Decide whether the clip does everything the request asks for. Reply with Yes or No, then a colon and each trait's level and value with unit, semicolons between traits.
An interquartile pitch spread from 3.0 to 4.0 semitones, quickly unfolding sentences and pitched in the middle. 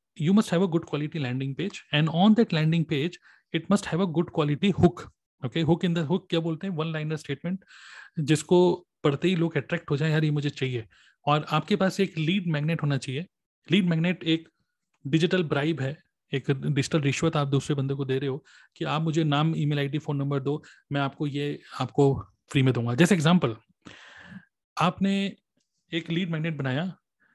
Yes: average, 3.5 semitones; fast, 195 wpm; medium, 160 Hz